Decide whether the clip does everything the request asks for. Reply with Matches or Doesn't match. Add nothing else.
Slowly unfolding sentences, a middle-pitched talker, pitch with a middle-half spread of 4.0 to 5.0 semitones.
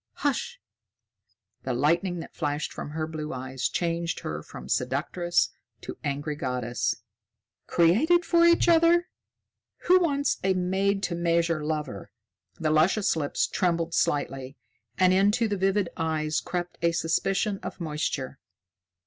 Matches